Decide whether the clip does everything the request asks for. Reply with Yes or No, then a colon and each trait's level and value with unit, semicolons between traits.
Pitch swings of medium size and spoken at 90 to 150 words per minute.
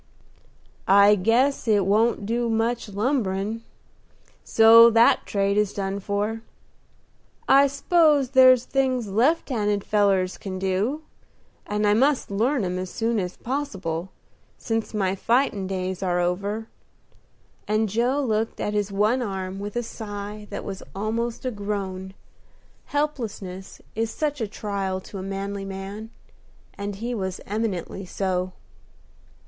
Yes: average, 3.2 semitones; slow, 135 wpm